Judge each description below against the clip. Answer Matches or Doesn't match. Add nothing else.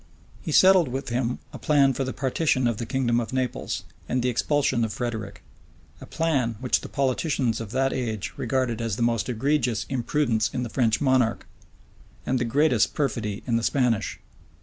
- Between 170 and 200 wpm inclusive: Matches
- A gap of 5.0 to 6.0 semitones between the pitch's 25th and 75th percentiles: Doesn't match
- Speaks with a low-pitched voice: Matches